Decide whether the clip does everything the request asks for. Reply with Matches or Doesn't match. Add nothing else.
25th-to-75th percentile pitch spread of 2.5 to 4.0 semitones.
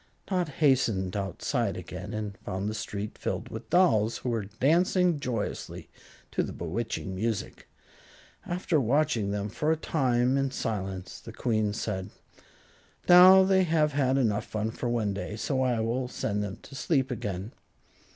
Doesn't match